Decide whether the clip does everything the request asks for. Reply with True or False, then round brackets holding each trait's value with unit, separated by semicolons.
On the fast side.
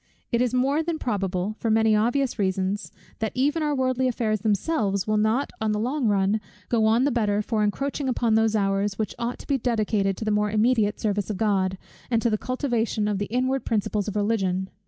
True (210 wpm)